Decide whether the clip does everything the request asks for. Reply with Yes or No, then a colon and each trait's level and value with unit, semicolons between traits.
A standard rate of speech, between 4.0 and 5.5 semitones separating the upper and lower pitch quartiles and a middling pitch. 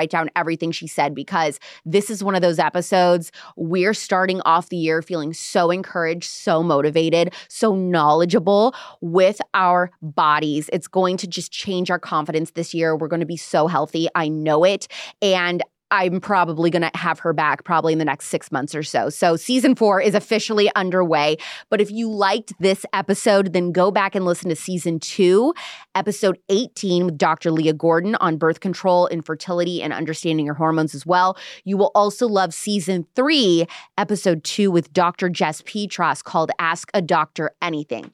No: average, 180 wpm; average, 3.2 semitones; medium, 175 Hz